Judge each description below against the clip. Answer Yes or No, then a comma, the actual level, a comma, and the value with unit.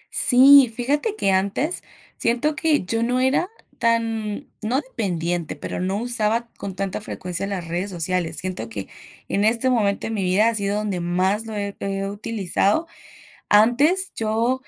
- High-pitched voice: Yes, high, 215 Hz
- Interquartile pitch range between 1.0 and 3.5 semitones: No, average, 4.1 semitones